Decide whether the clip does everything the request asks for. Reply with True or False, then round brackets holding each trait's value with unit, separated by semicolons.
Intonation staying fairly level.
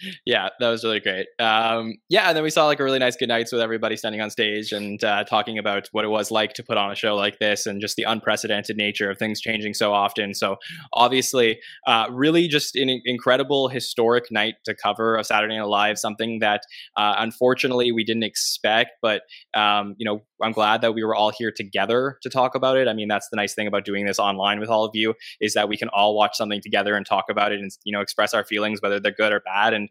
True (2.1 semitones)